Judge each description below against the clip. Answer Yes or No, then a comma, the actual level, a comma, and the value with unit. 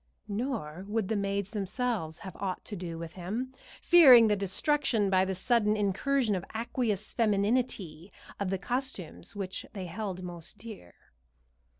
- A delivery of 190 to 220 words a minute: No, average, 150 wpm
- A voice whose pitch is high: Yes, high, 200 Hz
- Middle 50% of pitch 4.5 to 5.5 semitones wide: No, average, 3.8 semitones